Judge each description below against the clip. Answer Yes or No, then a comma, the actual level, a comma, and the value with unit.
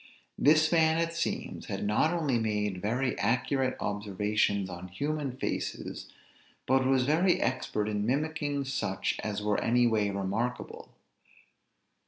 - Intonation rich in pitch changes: Yes, wide, 5.8 semitones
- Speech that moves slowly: Yes, slow, 130 wpm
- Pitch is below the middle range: Yes, low, 125 Hz